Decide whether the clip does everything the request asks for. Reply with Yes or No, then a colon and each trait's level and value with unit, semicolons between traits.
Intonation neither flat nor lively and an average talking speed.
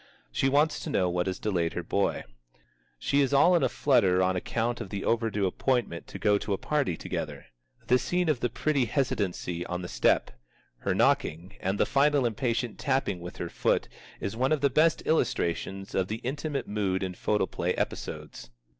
No: wide, 6.7 semitones; average, 190 wpm